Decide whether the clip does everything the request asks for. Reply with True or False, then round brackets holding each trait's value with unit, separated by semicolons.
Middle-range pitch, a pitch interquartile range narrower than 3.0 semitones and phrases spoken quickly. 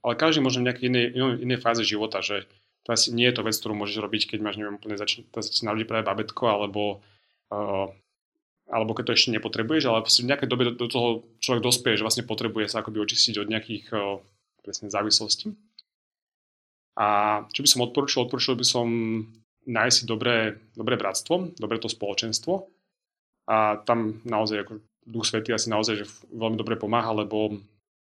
False (110 Hz; 2.4 semitones; 180 wpm)